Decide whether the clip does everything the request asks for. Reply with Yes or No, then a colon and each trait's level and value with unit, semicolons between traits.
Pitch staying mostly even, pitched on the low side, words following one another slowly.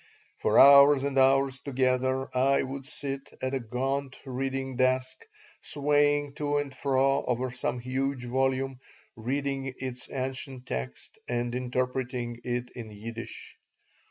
Yes: narrow, 1.6 semitones; low, 130 Hz; slow, 130 wpm